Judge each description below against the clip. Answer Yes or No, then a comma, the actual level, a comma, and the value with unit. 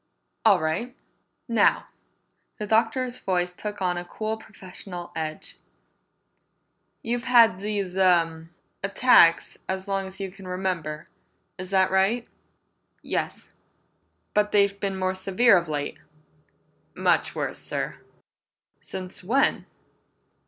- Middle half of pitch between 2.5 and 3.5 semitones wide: Yes, average, 2.8 semitones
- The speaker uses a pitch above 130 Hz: Yes, high, 190 Hz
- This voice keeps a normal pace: No, slow, 115 wpm